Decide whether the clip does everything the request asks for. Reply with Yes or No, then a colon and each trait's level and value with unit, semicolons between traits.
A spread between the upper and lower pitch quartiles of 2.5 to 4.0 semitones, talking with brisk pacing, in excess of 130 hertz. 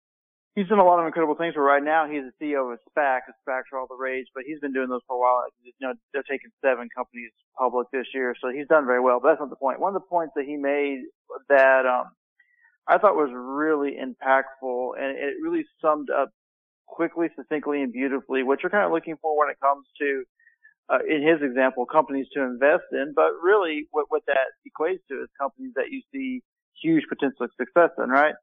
No: average, 4.4 semitones; fast, 225 wpm; medium, 140 Hz